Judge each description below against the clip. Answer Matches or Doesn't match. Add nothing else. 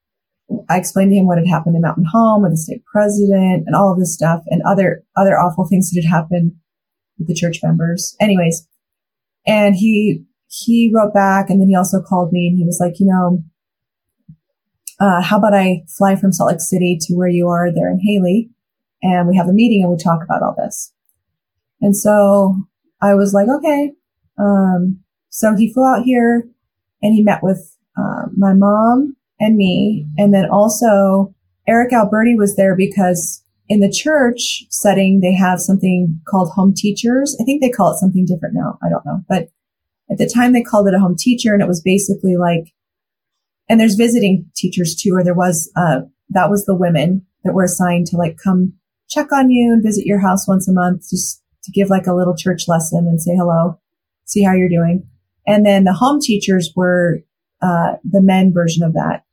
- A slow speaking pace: Doesn't match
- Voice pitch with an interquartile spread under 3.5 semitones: Matches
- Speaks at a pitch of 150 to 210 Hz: Matches